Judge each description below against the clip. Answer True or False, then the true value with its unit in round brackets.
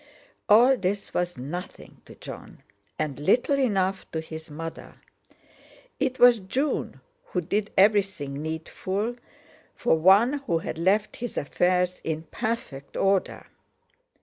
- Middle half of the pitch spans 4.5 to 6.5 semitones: True (5.1 semitones)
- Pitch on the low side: False (190 Hz)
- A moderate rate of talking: False (120 wpm)